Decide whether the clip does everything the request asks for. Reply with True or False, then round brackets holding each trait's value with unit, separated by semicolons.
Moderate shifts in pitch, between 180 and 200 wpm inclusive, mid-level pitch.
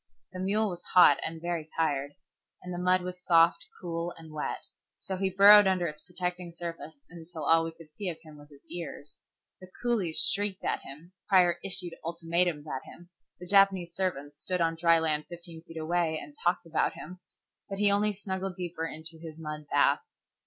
False (2.3 semitones; 190 wpm; 170 Hz)